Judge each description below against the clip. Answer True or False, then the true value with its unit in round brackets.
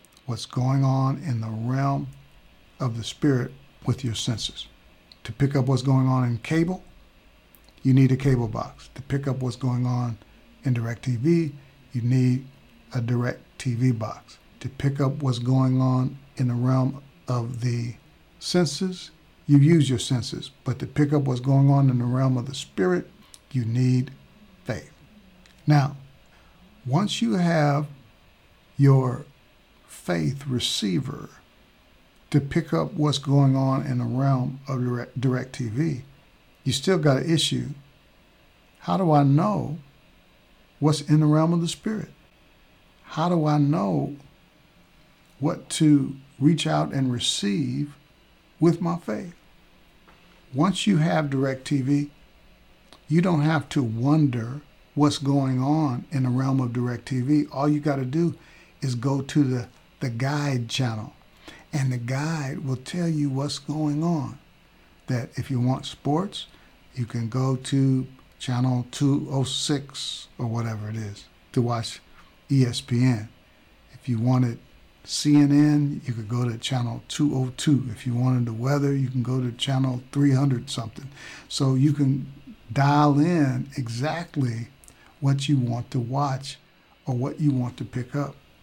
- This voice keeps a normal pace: True (150 wpm)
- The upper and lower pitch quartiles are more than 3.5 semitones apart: False (2.9 semitones)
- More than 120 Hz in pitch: True (135 Hz)